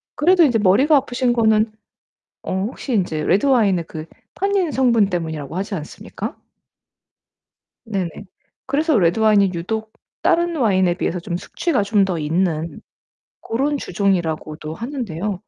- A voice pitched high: Yes, high, 205 Hz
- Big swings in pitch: Yes, wide, 6.6 semitones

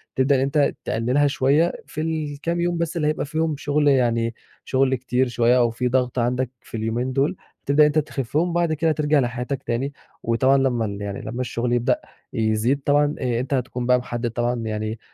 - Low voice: Yes, low, 130 Hz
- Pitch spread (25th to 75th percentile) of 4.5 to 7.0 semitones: No, average, 3.6 semitones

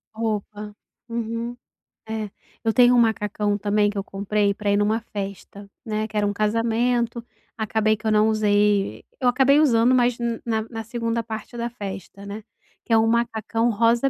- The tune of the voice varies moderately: No, narrow, 2.0 semitones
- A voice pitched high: Yes, high, 220 Hz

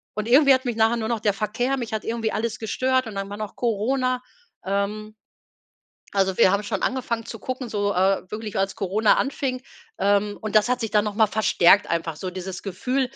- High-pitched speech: Yes, high, 215 Hz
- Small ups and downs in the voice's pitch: No, average, 3.3 semitones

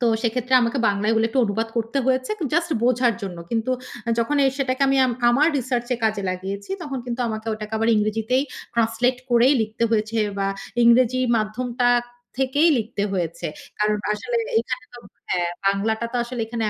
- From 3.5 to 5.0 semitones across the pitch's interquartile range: No, average, 2.9 semitones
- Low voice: No, high, 235 Hz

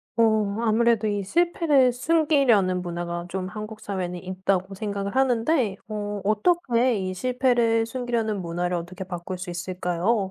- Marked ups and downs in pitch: No, average, 4.6 semitones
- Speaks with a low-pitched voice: No, high, 205 Hz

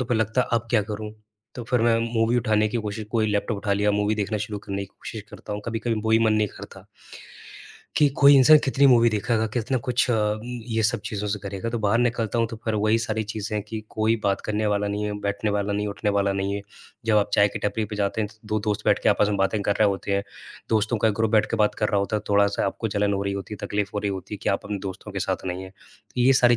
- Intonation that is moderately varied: No, narrow, 1.8 semitones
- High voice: No, low, 105 Hz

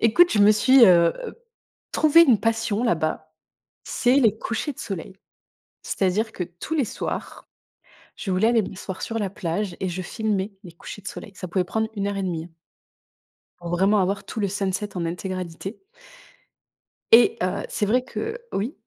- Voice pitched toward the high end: Yes, high, 200 Hz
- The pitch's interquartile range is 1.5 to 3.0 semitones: No, average, 3.7 semitones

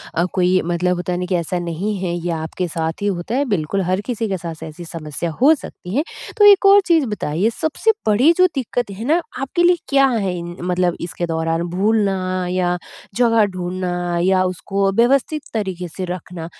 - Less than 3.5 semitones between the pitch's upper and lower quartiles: No, average, 4.6 semitones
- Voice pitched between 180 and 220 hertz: Yes, medium, 185 Hz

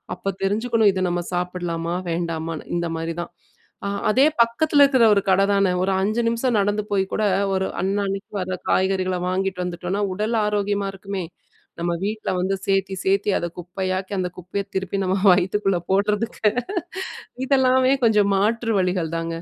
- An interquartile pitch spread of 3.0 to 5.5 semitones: No, narrow, 2.5 semitones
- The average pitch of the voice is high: Yes, high, 195 Hz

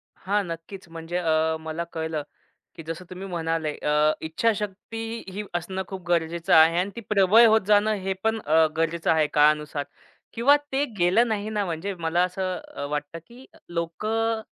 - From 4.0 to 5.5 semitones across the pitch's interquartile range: Yes, average, 4.4 semitones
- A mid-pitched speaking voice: Yes, medium, 175 Hz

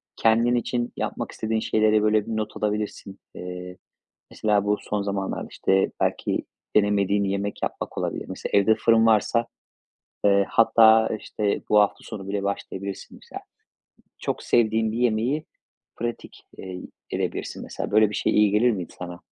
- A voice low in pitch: Yes, low, 105 Hz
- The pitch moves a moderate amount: No, narrow, 1.9 semitones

